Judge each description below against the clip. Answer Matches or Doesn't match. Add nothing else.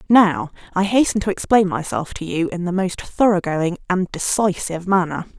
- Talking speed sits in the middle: Matches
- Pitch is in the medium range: Matches